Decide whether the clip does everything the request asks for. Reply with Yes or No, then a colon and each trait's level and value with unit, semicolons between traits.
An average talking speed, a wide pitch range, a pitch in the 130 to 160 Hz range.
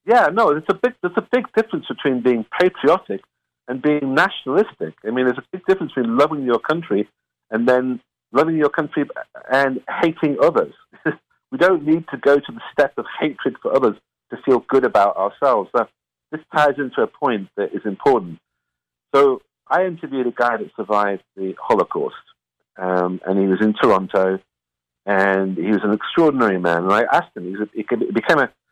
Yes: average, 180 wpm; wide, 8.9 semitones; medium, 140 Hz